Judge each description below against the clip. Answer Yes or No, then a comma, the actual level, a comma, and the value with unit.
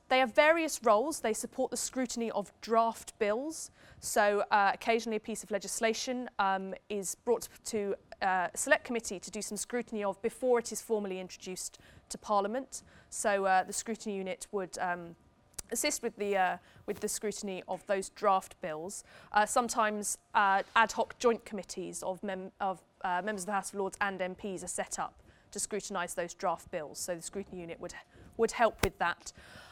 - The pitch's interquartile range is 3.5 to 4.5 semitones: No, average, 3.1 semitones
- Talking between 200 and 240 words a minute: No, average, 185 wpm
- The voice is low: No, high, 205 Hz